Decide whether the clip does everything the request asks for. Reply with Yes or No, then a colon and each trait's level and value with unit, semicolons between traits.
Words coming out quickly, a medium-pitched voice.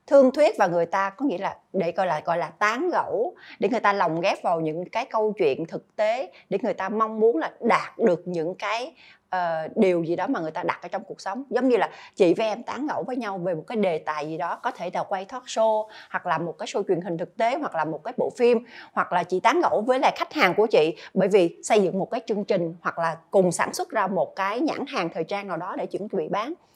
No: fast, 280 wpm; high, 210 Hz